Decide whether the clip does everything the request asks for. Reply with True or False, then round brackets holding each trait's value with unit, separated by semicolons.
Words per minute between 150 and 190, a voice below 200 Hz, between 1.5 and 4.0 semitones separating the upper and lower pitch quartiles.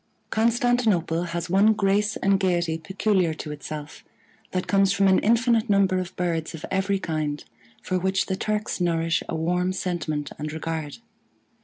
True (155 wpm; 185 Hz; 3.4 semitones)